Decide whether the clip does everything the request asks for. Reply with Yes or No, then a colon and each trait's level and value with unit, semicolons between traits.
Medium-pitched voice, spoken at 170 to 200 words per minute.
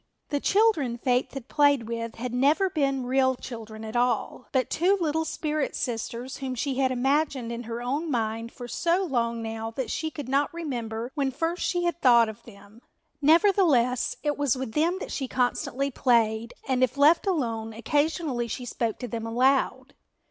No: very high, 255 Hz; average, 180 wpm